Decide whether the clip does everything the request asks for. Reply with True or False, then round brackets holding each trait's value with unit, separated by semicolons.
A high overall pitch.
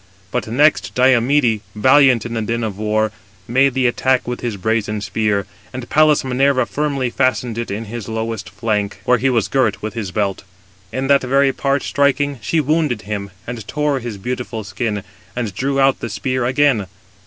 False (120 Hz)